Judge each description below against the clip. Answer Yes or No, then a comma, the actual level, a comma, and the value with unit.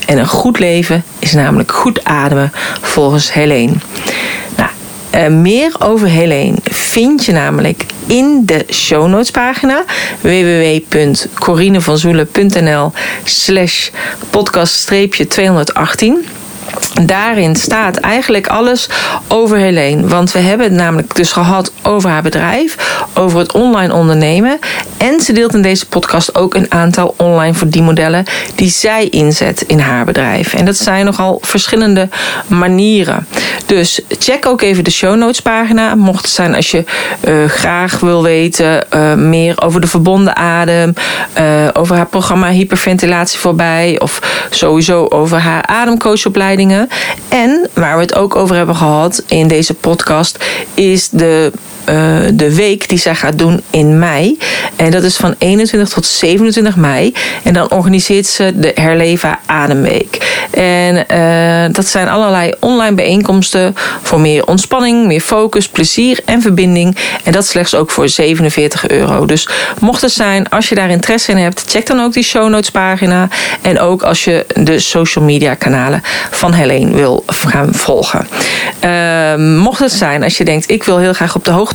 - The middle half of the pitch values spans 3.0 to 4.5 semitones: Yes, average, 4.2 semitones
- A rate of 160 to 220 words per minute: No, average, 150 wpm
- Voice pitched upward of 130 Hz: Yes, medium, 185 Hz